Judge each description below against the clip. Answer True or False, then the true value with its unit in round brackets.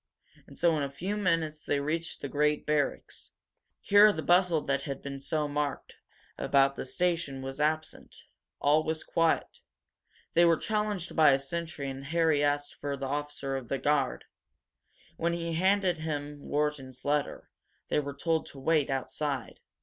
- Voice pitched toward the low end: False (150 Hz)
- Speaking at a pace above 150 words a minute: True (170 wpm)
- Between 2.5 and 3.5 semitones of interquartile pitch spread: True (2.9 semitones)